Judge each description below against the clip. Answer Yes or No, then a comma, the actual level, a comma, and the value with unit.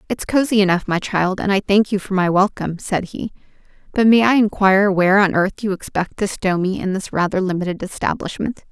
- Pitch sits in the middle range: No, high, 195 Hz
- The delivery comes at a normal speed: No, fast, 215 wpm